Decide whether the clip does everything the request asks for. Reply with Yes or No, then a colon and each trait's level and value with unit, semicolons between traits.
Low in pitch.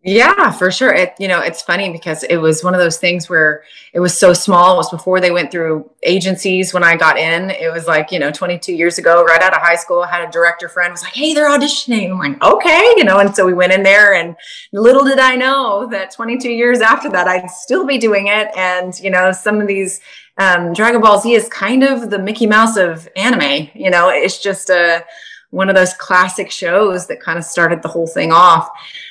No: medium, 185 Hz